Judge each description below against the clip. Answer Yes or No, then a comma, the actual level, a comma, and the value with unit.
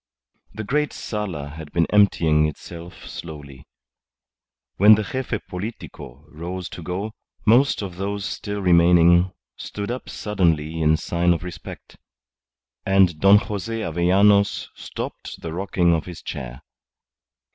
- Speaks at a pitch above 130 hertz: No, very low, 90 Hz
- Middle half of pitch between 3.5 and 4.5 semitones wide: Yes, average, 3.8 semitones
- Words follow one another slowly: Yes, slow, 125 wpm